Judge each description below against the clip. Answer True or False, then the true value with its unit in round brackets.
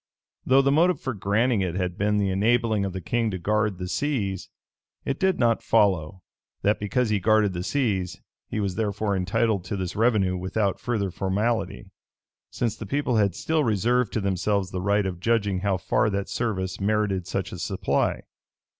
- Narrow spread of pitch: False (3.3 semitones)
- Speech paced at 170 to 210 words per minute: True (180 wpm)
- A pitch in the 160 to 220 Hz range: False (105 Hz)